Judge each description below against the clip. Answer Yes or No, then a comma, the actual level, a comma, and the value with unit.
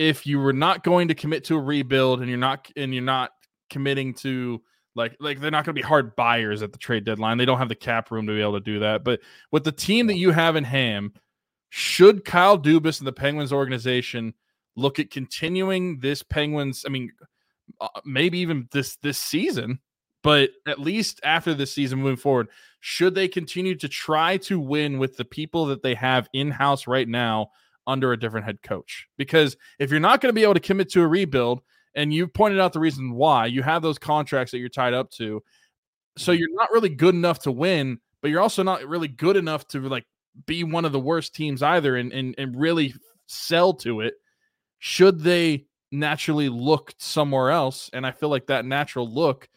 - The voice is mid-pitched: Yes, medium, 145 Hz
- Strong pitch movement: No, average, 4.3 semitones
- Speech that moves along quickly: Yes, fast, 210 wpm